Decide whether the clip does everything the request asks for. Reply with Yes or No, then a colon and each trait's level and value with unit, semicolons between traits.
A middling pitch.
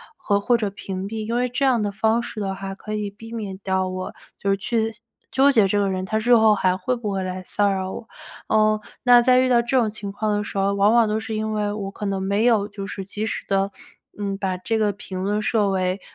No: high, 205 Hz